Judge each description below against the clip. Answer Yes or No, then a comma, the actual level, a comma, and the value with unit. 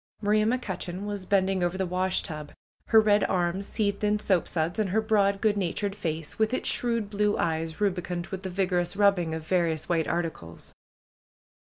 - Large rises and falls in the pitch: No, average, 3.1 semitones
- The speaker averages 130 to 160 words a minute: No, average, 170 wpm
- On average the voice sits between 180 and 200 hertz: Yes, high, 190 Hz